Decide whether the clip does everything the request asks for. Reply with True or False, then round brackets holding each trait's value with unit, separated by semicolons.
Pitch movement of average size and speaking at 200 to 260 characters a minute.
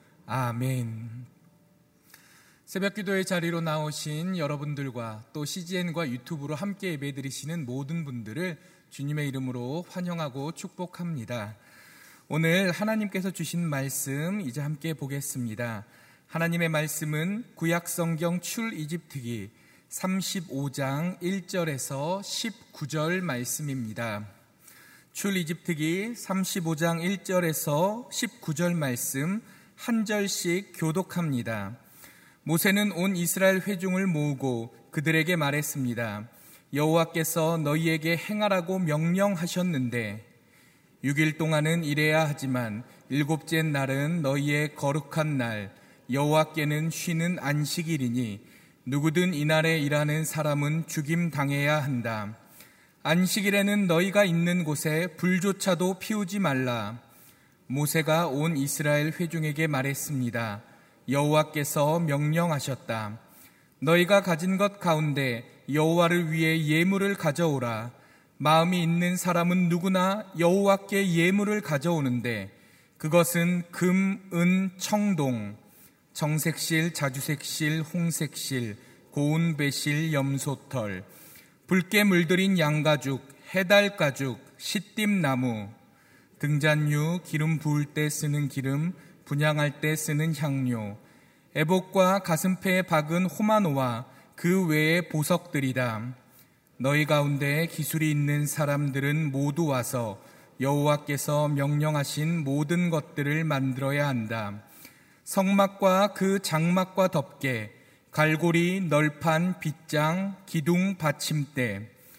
True (4.1 semitones; 240 characters per minute)